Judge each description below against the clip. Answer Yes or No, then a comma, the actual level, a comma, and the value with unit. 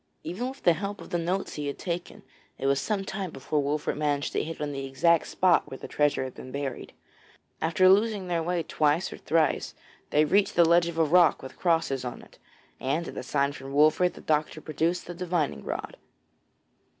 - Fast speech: Yes, fast, 210 wpm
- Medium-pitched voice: Yes, medium, 160 Hz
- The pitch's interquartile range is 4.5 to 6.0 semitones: No, average, 3.6 semitones